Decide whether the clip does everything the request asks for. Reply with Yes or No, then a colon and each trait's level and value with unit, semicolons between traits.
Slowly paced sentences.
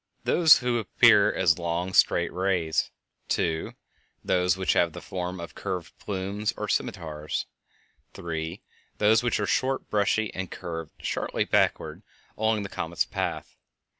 No: average, 145 wpm